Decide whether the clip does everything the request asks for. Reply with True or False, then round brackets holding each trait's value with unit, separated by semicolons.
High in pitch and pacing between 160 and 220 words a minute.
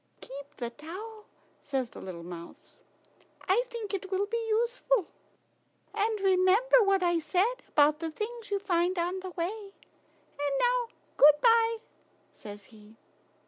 False (380 Hz; 140 wpm)